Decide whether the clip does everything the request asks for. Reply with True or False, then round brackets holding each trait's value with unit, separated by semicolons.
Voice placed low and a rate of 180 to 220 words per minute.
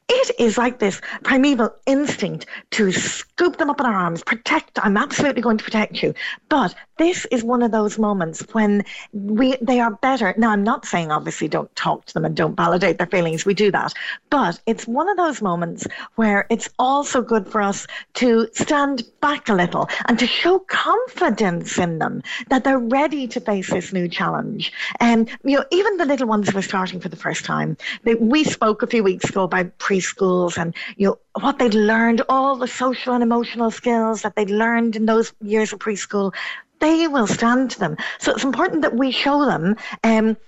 False (230 Hz; 200 wpm)